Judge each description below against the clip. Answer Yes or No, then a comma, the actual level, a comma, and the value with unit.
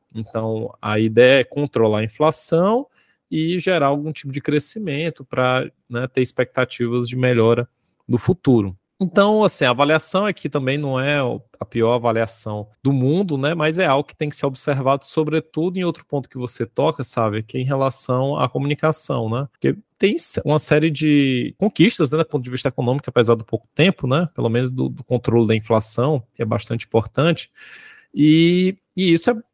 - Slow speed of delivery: No, fast, 185 wpm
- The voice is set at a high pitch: No, low, 135 Hz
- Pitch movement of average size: Yes, average, 4.7 semitones